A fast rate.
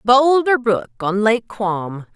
No: average, 140 wpm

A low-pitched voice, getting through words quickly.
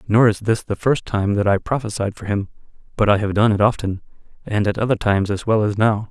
Yes: low, 105 Hz; fast, 245 wpm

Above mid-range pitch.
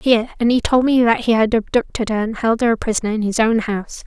Yes: high, 225 Hz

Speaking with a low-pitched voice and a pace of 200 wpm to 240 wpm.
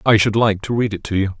No: low, 105 Hz; fast, 345 wpm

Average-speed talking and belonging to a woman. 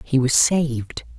Yes: average, 150 wpm; female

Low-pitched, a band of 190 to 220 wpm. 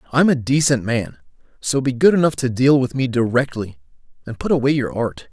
Yes: low, 130 Hz; fast, 205 wpm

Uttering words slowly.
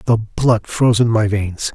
No: fast, 205 wpm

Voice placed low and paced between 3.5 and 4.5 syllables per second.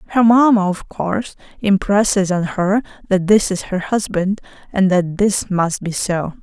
No: high, 195 Hz; 4.4 syllables/s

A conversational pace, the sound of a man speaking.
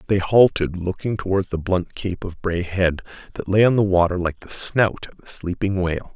No: fast, 215 wpm; male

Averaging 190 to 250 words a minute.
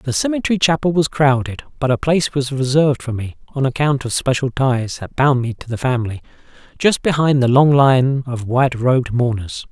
Yes: average, 200 wpm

